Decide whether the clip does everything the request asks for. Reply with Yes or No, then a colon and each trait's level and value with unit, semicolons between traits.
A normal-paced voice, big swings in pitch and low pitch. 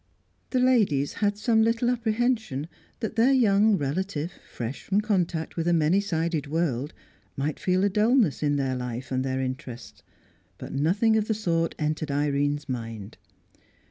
No: average, 155 wpm; wide, 7.3 semitones; medium, 165 Hz